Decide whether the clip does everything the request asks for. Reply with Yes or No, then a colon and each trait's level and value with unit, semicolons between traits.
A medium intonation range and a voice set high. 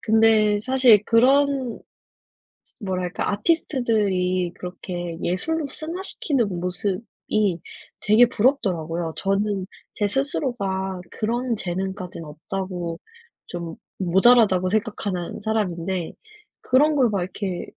Yes: average, 4.8 semitones; high, 200 Hz